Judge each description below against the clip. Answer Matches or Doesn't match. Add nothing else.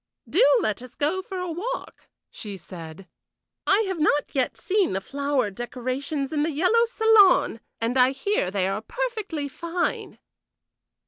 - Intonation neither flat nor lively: Doesn't match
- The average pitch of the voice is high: Matches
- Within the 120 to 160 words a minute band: Matches